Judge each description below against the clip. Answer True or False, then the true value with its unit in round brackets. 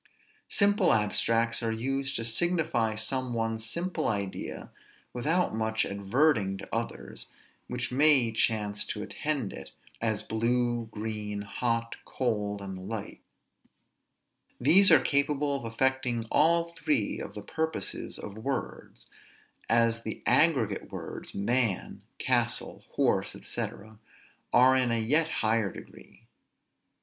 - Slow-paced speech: True (120 wpm)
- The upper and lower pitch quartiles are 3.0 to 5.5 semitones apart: True (3.9 semitones)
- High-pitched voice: False (115 Hz)